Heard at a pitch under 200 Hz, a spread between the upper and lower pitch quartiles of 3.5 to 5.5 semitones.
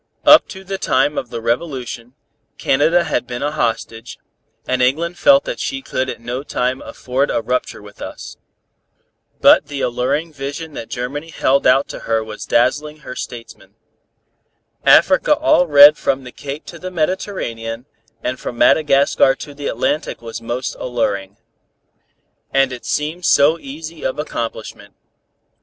Yes: low, 135 Hz; average, 4.0 semitones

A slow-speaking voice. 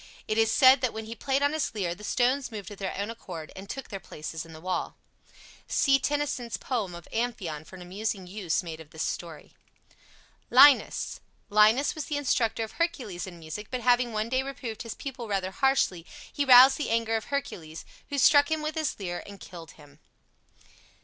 No: average, 200 wpm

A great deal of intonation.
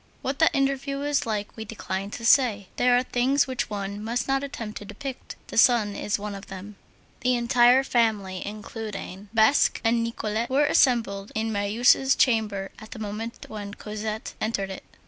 No: average, 3.4 semitones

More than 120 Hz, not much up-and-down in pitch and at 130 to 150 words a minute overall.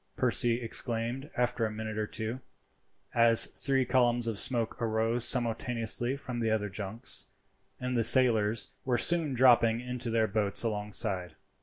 No: low, 115 Hz; narrow, 2.1 semitones; average, 145 wpm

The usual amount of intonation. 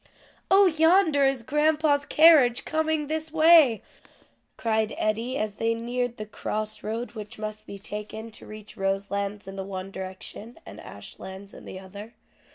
No: wide, 6.2 semitones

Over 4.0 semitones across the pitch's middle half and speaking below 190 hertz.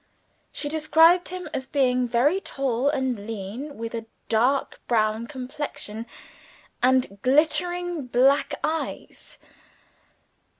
No: average, 4.6 semitones; very high, 260 Hz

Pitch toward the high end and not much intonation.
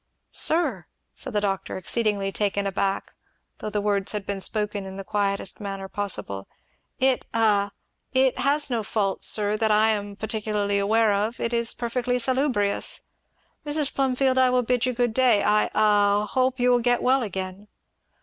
No: high, 215 Hz; average, 3.6 semitones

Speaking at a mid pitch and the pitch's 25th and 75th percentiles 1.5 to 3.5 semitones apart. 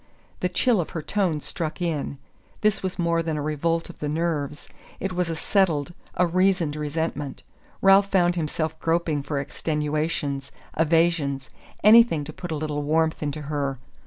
Yes: medium, 160 Hz; average, 2.9 semitones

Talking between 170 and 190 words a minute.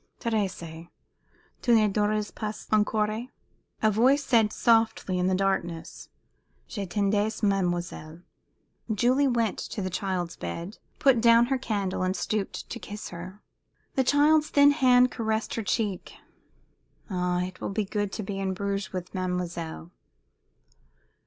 No: average, 140 wpm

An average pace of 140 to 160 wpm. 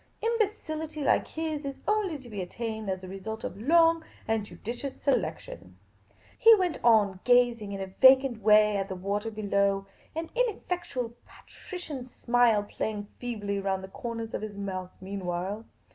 Yes: average, 155 wpm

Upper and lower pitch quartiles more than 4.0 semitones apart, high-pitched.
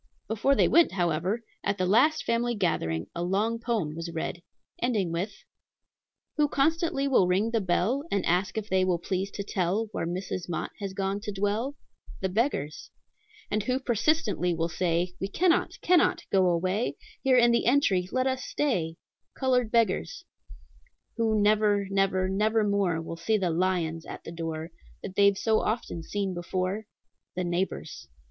Yes: average, 4.5 semitones; high, 200 Hz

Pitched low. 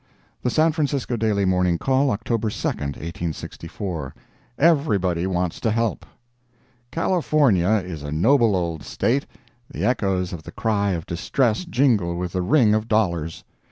Yes: low, 100 Hz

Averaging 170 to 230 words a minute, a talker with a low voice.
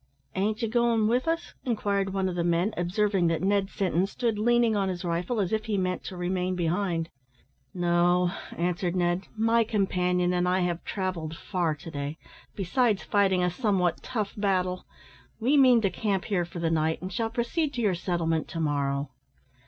No: average, 185 wpm; medium, 185 Hz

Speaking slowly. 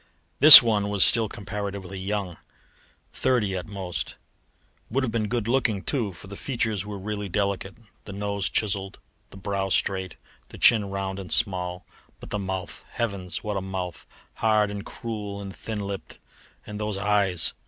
No: average, 165 wpm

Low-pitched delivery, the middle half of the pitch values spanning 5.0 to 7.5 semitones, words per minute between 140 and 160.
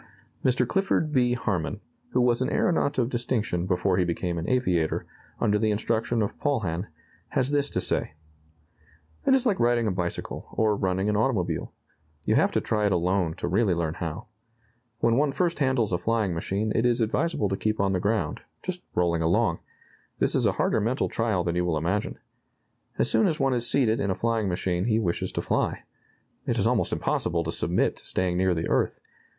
No: low, 105 Hz; wide, 5.5 semitones; average, 200 wpm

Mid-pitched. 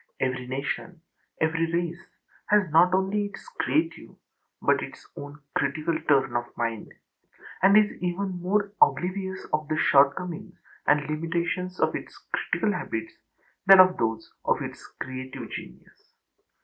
Yes: medium, 165 Hz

